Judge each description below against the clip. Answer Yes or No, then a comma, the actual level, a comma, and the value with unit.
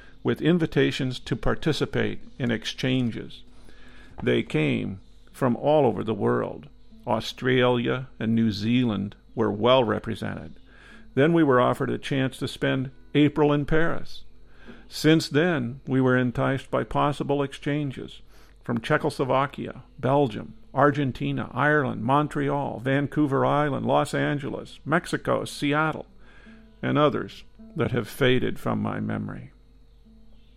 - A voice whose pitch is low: Yes, low, 130 Hz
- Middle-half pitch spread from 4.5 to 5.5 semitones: No, average, 3.4 semitones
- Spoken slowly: Yes, slow, 115 wpm